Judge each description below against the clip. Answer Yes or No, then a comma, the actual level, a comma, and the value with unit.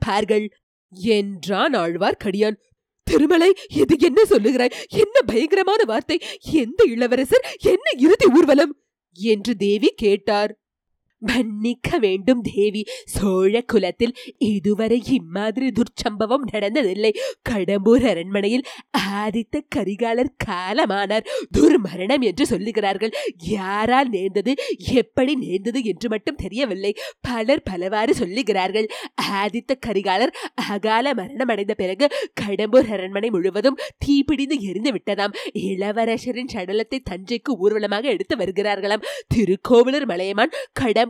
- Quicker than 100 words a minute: No, average, 95 wpm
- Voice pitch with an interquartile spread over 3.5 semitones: Yes, wide, 5.5 semitones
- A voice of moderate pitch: No, high, 235 Hz